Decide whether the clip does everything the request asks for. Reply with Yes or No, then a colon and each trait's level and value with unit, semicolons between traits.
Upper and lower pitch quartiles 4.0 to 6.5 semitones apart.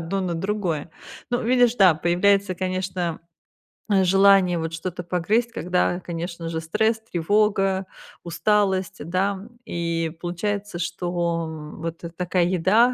No: average, 2.8 semitones